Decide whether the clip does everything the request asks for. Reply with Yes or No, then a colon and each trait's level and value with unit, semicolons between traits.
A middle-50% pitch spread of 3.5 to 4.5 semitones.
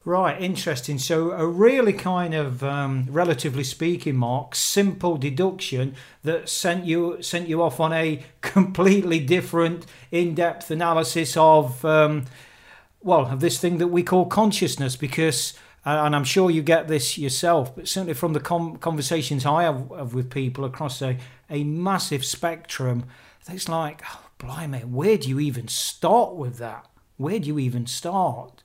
Yes: average, 3.9 semitones